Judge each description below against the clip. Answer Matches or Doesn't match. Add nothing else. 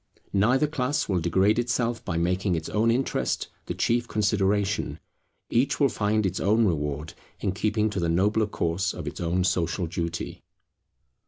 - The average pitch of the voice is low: Matches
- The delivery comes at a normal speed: Matches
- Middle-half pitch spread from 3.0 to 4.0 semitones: Doesn't match